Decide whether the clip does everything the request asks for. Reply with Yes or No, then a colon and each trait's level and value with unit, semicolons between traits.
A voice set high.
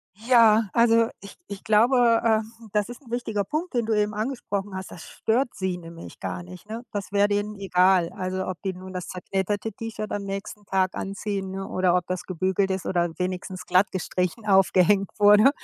Yes: high, 200 Hz